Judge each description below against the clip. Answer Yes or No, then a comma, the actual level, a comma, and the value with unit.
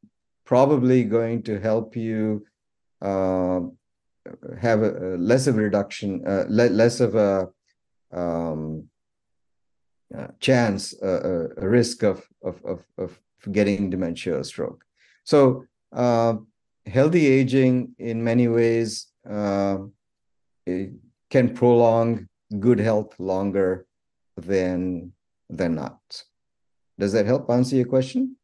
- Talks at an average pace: No, slow, 115 wpm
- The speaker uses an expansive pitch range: No, average, 4.0 semitones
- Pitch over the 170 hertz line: No, low, 110 Hz